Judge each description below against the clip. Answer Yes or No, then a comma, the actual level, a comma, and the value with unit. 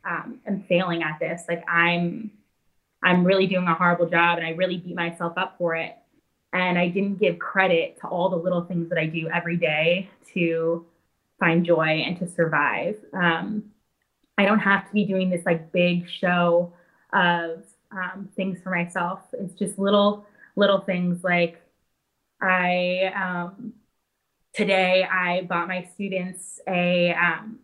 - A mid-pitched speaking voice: Yes, medium, 180 Hz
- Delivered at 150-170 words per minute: Yes, average, 160 wpm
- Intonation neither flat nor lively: No, narrow, 2.0 semitones